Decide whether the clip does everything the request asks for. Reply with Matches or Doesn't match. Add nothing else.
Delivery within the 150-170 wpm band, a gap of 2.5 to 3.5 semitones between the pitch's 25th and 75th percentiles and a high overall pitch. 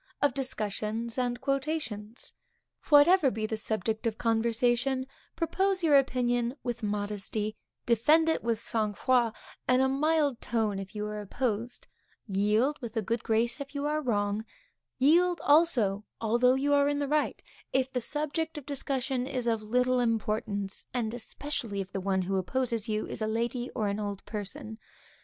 Doesn't match